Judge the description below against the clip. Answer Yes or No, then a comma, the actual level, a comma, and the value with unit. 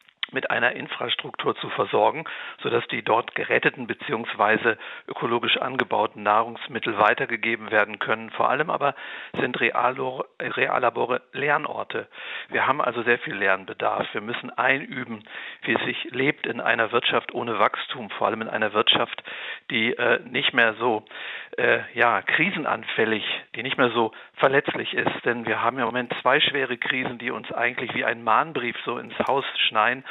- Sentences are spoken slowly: No, average, 155 wpm